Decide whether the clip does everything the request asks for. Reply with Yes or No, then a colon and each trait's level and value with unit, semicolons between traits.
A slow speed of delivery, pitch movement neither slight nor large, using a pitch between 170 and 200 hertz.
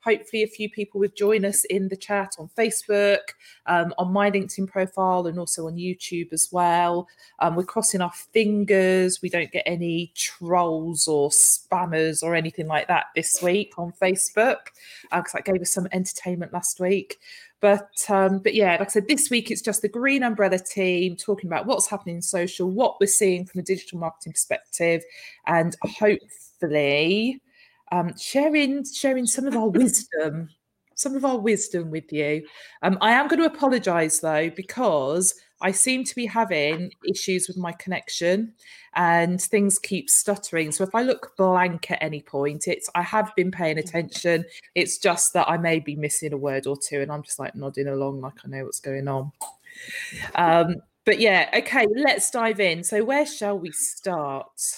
No: average, 180 wpm; average, 3.9 semitones; medium, 185 Hz